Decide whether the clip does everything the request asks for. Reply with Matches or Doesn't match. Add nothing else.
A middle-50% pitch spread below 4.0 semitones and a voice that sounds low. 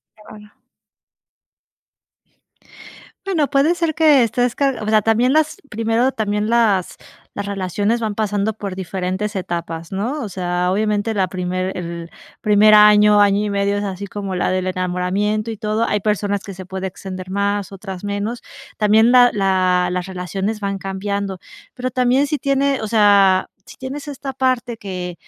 Doesn't match